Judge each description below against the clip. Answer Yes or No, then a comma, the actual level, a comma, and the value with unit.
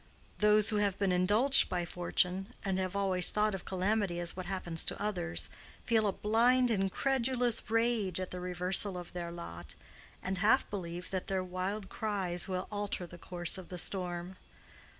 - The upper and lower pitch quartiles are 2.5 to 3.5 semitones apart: Yes, average, 2.8 semitones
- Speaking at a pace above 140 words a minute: Yes, average, 170 wpm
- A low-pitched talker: No, high, 190 Hz